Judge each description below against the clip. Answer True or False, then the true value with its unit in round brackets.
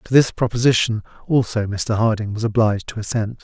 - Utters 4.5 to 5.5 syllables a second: False (5.8 syllables/s)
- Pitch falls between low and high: False (110 Hz)